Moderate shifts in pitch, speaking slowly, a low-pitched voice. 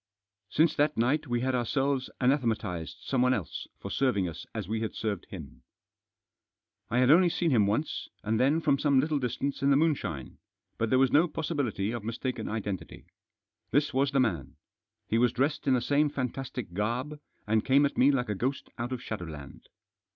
No: average, 4.3 semitones; average, 185 wpm; low, 125 Hz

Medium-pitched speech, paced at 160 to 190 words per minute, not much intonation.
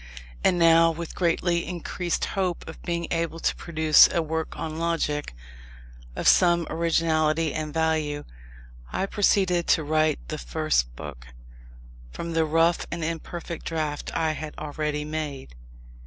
No: medium, 160 Hz; average, 140 wpm; narrow, 1.7 semitones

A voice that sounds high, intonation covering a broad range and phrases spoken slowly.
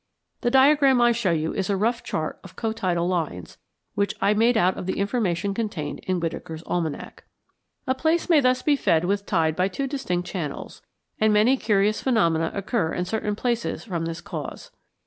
No: high, 200 Hz; wide, 5.7 semitones; average, 185 wpm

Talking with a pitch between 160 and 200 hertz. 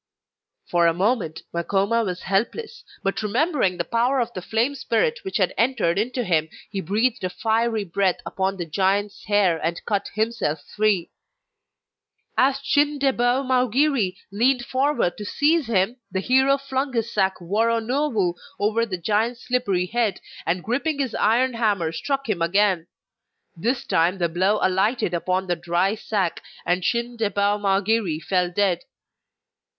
No: high, 210 Hz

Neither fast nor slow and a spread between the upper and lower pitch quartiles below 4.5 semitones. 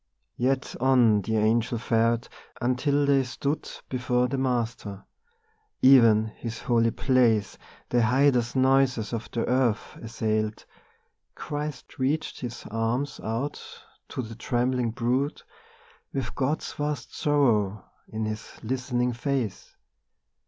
No: slow, 115 wpm; average, 2.9 semitones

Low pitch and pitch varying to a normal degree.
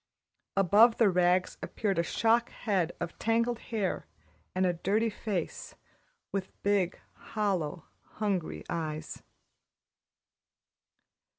No: high, 195 Hz; average, 3.7 semitones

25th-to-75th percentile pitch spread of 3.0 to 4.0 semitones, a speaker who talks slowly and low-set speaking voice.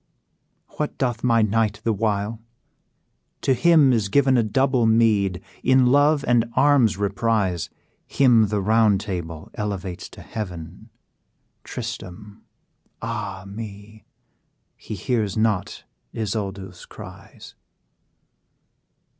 Yes: average, 3.3 semitones; slow, 105 wpm; low, 110 Hz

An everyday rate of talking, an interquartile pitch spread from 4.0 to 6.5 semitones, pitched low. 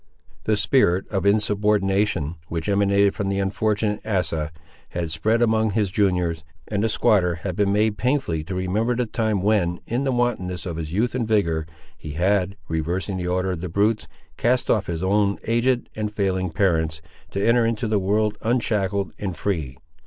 No: average, 175 wpm; average, 3.4 semitones; low, 100 Hz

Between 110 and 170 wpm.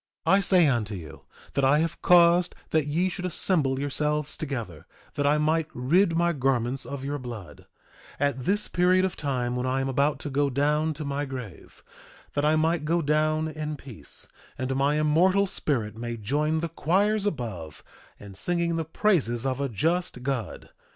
No: average, 180 wpm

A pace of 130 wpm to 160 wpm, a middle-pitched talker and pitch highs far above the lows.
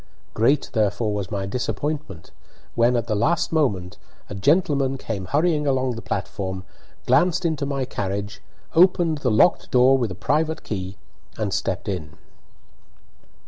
No: average, 145 wpm; low, 120 Hz; wide, 6.8 semitones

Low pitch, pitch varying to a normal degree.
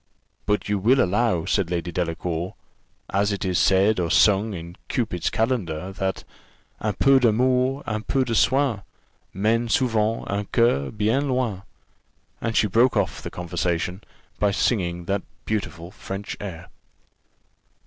Yes: low, 100 Hz; average, 4.3 semitones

